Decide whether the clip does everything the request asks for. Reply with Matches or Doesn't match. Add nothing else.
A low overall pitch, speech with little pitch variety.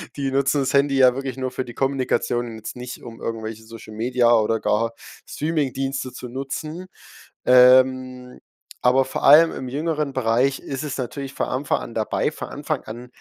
Matches